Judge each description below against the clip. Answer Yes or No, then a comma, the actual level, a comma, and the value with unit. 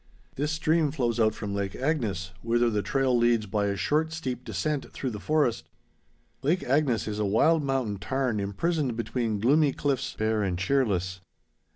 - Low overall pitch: Yes, low, 120 Hz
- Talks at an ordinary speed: Yes, average, 170 wpm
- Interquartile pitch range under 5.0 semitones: No, wide, 5.4 semitones